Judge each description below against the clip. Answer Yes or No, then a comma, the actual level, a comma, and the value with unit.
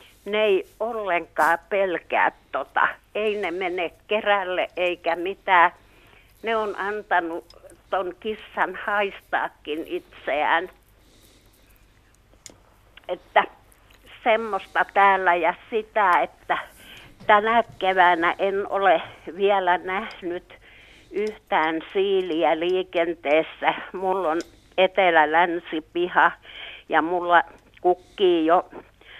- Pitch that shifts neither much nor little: Yes, average, 3.9 semitones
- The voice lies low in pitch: No, medium, 180 Hz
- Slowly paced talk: Yes, slow, 80 wpm